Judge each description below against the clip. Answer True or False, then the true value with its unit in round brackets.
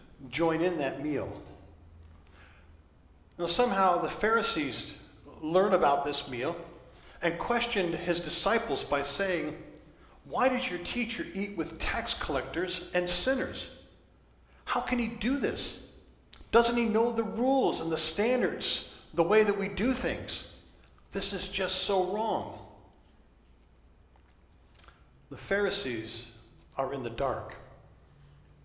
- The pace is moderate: False (120 wpm)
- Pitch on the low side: False (160 Hz)